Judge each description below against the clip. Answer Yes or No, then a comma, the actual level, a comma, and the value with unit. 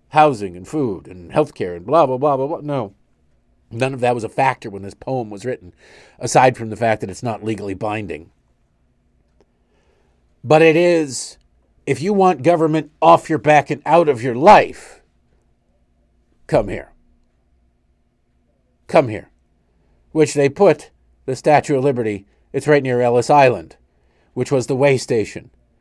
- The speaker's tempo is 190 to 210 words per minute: No, average, 160 wpm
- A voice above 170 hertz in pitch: No, low, 120 Hz